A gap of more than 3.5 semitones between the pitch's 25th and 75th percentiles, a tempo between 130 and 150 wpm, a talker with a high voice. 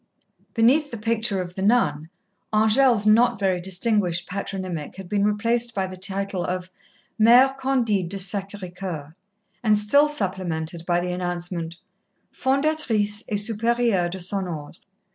Yes: average, 4.2 semitones; average, 140 wpm; high, 200 Hz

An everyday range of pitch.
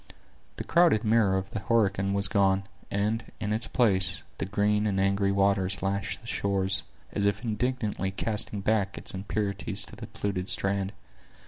No: narrow, 1.7 semitones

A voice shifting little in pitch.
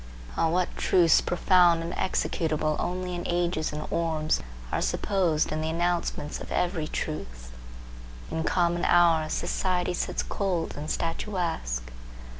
Yes: narrow, 2.2 semitones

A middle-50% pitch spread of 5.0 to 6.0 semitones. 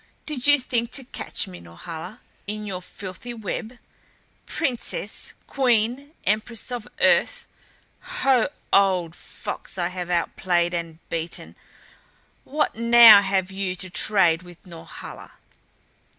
Yes: average, 5.3 semitones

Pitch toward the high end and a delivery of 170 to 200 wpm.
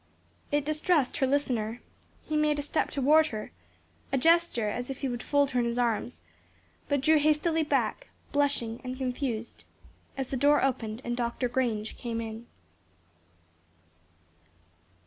No: very high, 260 Hz; average, 145 wpm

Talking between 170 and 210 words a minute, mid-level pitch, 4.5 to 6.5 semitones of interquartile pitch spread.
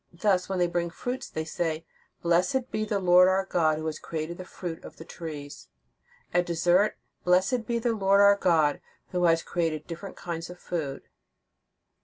No: average, 180 wpm; medium, 175 Hz; average, 2.8 semitones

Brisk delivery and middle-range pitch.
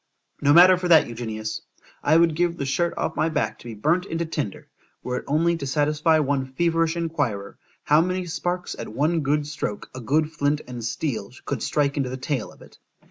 Yes: fast, 210 wpm; medium, 150 Hz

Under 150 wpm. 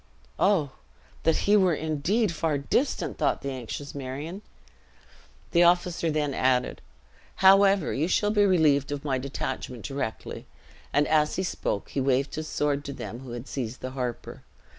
No: average, 160 wpm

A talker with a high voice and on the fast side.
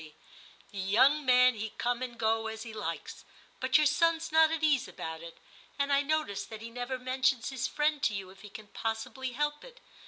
Yes: very high, 250 Hz; fast, 210 wpm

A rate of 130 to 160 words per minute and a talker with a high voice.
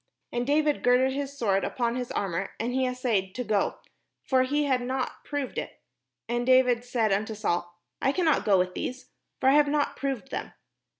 No: average, 190 wpm; very high, 250 Hz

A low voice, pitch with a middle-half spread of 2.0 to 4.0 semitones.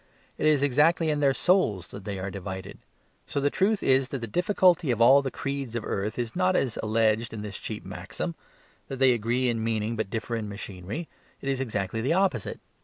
No: low, 120 Hz; average, 5.0 semitones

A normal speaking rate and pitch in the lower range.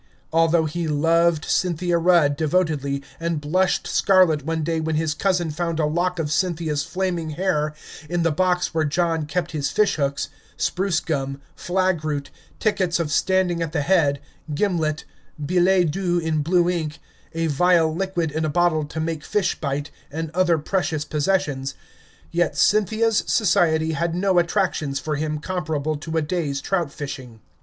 No: average, 160 wpm; medium, 165 Hz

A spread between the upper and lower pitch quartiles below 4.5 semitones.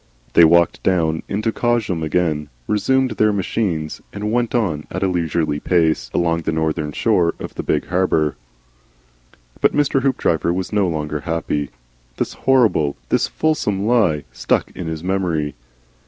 No: average, 5.1 semitones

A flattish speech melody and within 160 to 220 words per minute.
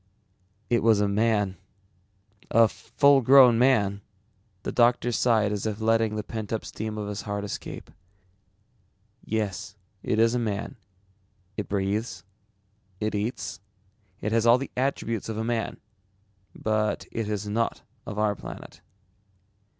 No: narrow, 1.9 semitones; average, 140 wpm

